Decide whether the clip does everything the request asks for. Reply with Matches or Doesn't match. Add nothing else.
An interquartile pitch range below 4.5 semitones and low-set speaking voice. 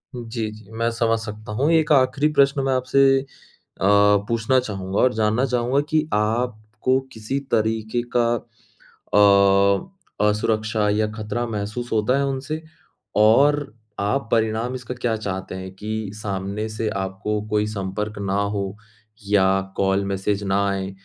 Matches